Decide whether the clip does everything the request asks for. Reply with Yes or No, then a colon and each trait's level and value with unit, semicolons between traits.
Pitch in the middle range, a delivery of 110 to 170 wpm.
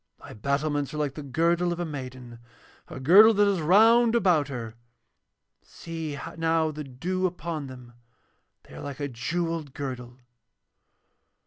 Yes: medium, 150 Hz; average, 145 wpm